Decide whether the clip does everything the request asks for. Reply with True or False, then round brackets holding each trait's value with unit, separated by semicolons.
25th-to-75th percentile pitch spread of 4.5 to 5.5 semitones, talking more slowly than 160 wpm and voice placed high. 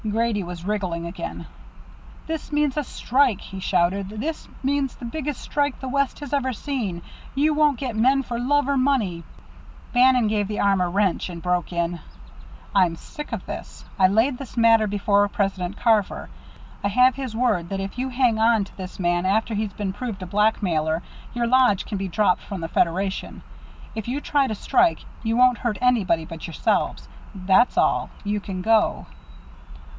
False (5.1 semitones; 180 wpm; 215 Hz)